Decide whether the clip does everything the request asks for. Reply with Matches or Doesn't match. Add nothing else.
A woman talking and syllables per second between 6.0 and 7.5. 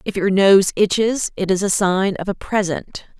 Doesn't match